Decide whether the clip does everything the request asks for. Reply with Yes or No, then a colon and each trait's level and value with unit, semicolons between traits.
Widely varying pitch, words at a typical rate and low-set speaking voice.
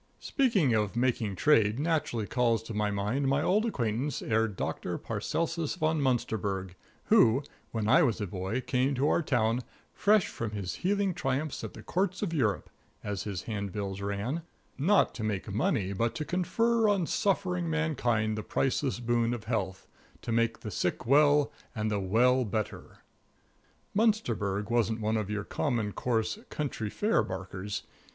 Yes: wide, 6.5 semitones; average, 160 wpm; low, 120 Hz